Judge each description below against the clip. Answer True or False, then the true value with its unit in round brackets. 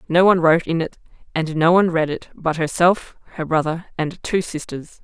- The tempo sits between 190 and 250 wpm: True (205 wpm)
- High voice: False (165 Hz)